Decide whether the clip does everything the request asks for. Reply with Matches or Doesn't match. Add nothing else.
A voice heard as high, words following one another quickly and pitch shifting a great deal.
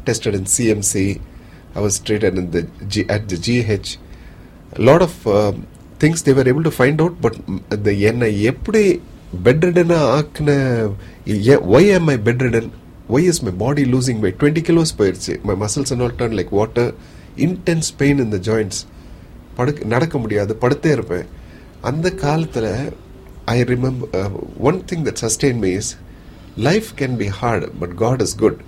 Doesn't match